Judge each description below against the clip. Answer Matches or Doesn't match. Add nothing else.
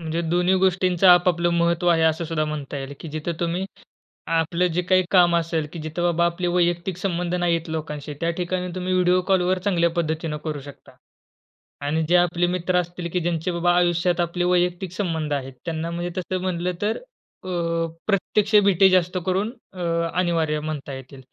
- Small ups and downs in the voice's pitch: Matches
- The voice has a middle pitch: Matches